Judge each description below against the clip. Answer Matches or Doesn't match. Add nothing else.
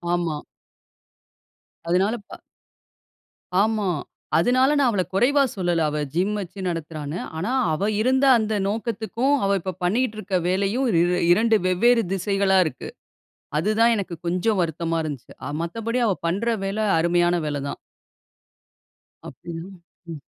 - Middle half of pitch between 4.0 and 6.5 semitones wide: Matches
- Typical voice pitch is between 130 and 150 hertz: Doesn't match